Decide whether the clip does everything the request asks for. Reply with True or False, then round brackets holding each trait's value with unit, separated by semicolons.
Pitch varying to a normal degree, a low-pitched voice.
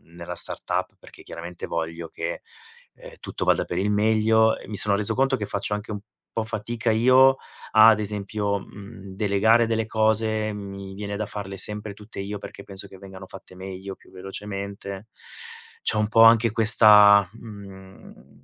False (2.0 semitones; 105 Hz)